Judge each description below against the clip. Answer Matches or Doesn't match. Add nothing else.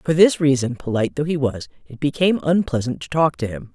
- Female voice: Matches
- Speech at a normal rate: Doesn't match